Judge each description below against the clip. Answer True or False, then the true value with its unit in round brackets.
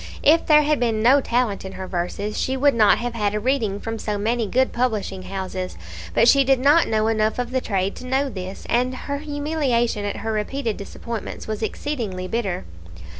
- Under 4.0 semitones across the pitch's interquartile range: False (4.3 semitones)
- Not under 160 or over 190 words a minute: False (200 wpm)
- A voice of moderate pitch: False (230 Hz)